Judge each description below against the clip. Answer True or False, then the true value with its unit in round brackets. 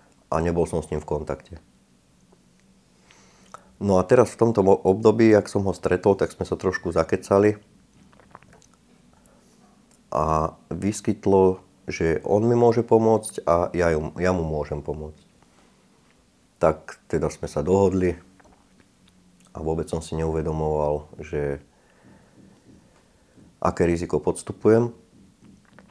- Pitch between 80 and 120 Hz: True (90 Hz)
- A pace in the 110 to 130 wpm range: True (115 wpm)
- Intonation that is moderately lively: True (4.3 semitones)